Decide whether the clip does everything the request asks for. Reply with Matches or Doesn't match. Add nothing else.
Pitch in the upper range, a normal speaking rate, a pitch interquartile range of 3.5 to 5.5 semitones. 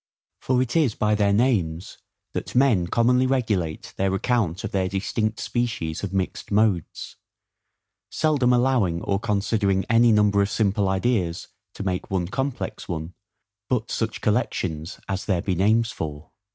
Doesn't match